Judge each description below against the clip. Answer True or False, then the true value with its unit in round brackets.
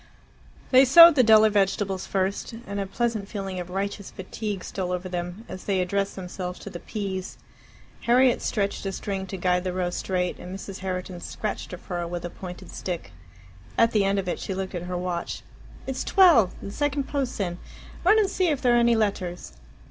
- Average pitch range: True (3.6 semitones)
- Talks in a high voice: True (195 Hz)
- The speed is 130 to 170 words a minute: False (200 wpm)